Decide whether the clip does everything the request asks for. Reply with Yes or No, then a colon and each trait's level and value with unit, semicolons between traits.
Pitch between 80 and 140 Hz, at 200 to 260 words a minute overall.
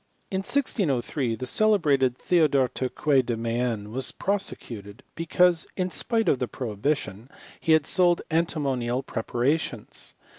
No: low, 135 Hz; slow, 135 wpm